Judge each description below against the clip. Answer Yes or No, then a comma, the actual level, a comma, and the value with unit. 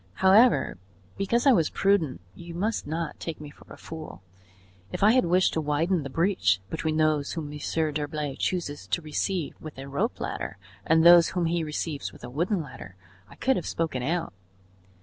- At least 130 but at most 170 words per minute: No, average, 190 wpm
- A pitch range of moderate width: Yes, average, 3.3 semitones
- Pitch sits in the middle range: Yes, medium, 160 Hz